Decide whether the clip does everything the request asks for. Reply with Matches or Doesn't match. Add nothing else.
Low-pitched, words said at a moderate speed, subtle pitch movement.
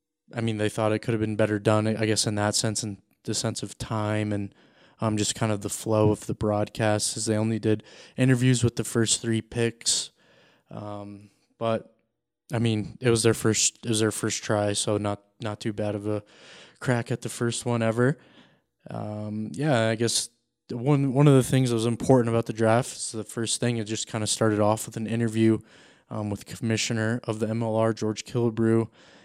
Doesn't match